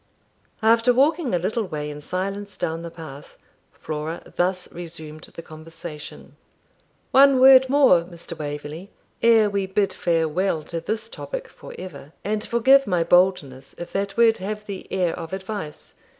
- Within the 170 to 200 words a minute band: No, average, 150 wpm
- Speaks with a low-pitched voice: No, medium, 185 Hz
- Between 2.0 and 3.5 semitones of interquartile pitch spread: No, average, 5.1 semitones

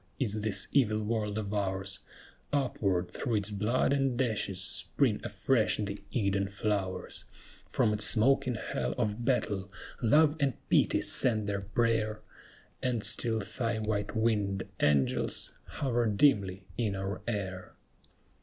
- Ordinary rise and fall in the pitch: Yes, average, 3.2 semitones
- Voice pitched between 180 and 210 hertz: No, low, 105 Hz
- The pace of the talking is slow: Yes, slow, 130 wpm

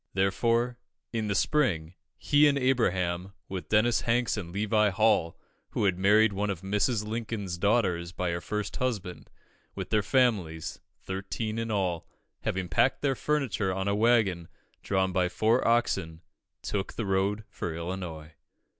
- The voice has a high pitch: No, low, 100 Hz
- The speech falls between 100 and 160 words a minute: Yes, average, 150 wpm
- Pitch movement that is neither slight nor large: Yes, average, 3.9 semitones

